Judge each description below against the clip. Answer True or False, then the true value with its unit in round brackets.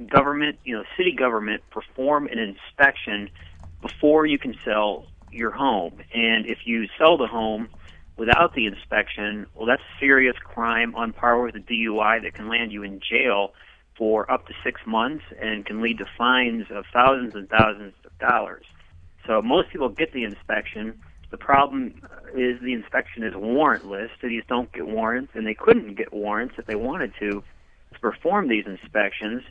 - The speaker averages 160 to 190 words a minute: True (170 wpm)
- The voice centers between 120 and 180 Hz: False (110 Hz)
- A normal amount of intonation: True (3.4 semitones)